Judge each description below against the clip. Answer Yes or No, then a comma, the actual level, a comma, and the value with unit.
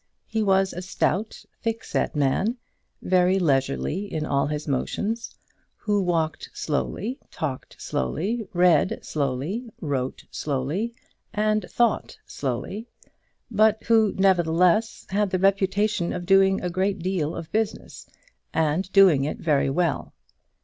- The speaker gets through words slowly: Yes, slow, 120 wpm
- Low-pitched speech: No, medium, 185 Hz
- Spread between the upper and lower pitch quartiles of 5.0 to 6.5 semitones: Yes, average, 5.3 semitones